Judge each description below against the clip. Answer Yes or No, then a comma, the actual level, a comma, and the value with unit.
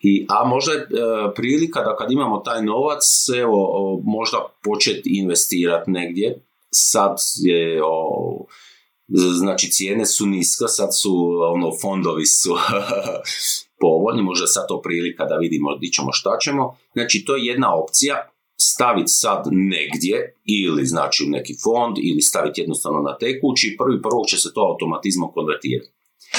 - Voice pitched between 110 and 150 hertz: No, low, 100 Hz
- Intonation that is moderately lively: No, wide, 8.8 semitones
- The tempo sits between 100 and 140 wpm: No, average, 150 wpm